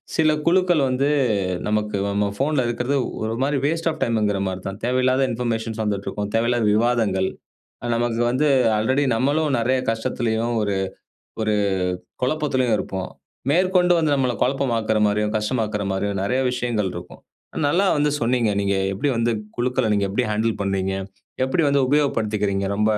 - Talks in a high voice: No, low, 115 Hz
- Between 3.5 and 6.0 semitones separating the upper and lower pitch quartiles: Yes, average, 4.3 semitones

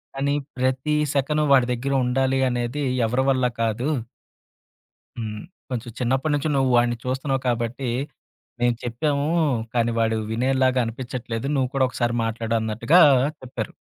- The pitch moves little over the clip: Yes, narrow, 2.2 semitones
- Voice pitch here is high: No, low, 125 Hz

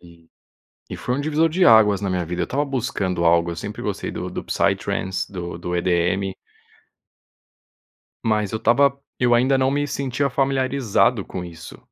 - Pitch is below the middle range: Yes, low, 110 Hz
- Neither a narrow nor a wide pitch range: No, wide, 7.2 semitones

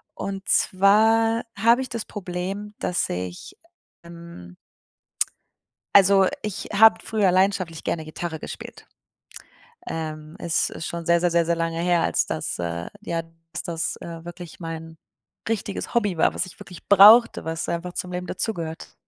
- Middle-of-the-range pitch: Yes, medium, 175 Hz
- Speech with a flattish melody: No, average, 3.5 semitones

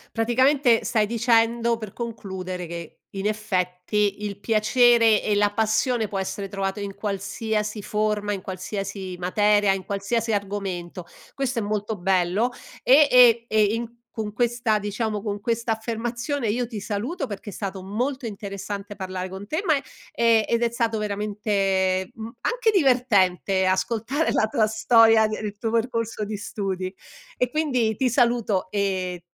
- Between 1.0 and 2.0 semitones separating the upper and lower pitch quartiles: No, average, 2.8 semitones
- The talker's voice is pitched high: Yes, high, 215 Hz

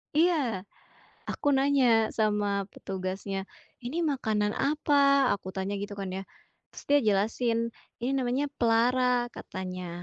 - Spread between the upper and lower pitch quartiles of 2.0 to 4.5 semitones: No, wide, 5.4 semitones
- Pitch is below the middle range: No, high, 230 Hz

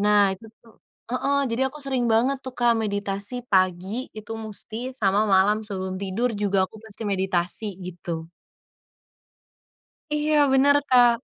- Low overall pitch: No, high, 215 Hz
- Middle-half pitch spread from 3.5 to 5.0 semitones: Yes, average, 4.2 semitones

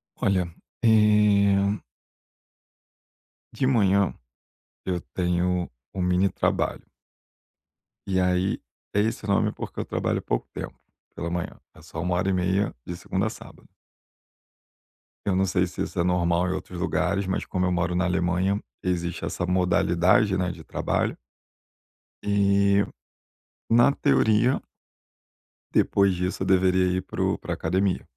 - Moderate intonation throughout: No, narrow, 1.9 semitones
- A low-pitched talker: Yes, very low, 95 Hz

